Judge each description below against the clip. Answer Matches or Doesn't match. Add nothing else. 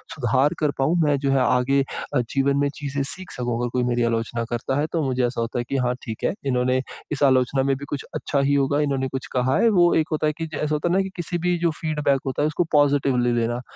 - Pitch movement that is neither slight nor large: Matches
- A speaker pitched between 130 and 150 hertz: Matches